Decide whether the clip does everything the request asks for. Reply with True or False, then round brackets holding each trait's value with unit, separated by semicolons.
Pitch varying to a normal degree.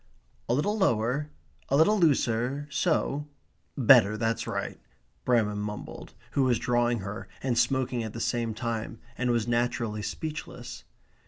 True (3.4 semitones)